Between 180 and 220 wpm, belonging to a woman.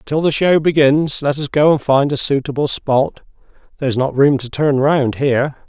No: average, 200 wpm; male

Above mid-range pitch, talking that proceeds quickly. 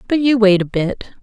Yes: high, 220 Hz; fast, 245 wpm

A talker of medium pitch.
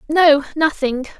No: very high, 295 Hz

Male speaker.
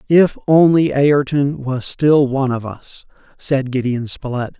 Yes: male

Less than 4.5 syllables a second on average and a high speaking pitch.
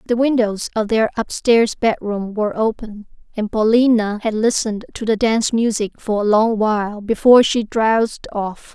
No: 4.9 syllables/s; high, 220 Hz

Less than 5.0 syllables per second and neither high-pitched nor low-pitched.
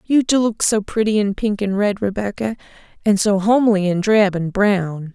No: 4.8 syllables/s; high, 205 Hz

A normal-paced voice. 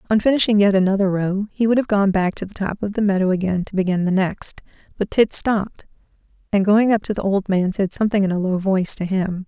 No: fast, 245 wpm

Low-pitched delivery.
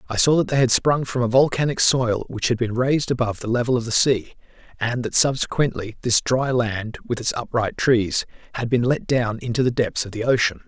Yes: low, 120 Hz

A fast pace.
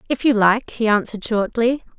No: average, 180 wpm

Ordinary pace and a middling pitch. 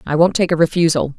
No: fast, 255 wpm; medium, 165 Hz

